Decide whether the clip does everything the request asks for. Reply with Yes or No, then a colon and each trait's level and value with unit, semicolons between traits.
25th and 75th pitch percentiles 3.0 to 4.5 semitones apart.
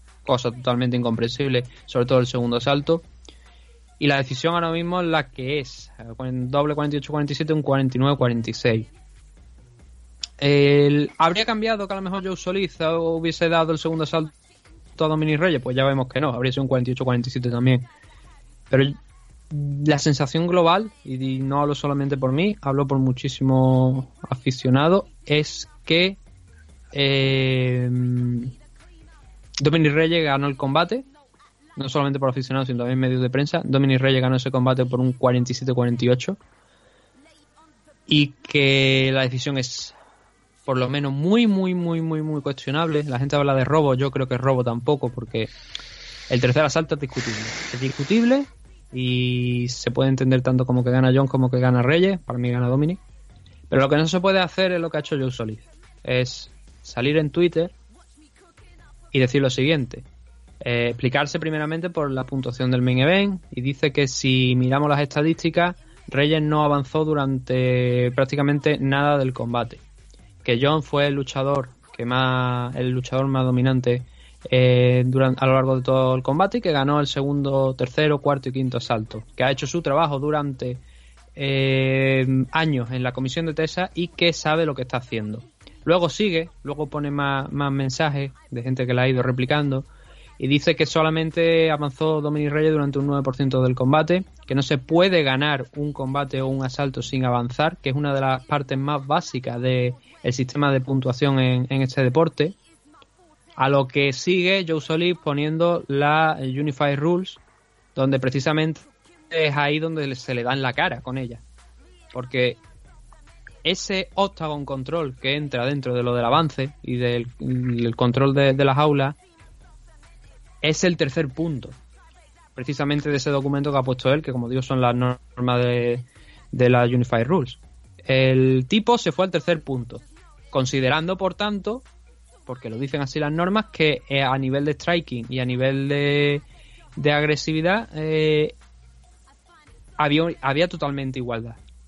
Yes: average, 3.4 semitones